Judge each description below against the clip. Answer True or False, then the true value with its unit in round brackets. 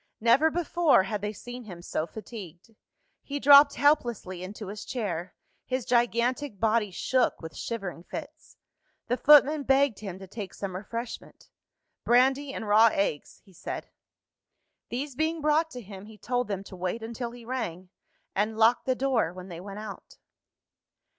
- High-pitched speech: True (230 Hz)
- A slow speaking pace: False (160 wpm)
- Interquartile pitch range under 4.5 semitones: False (5.0 semitones)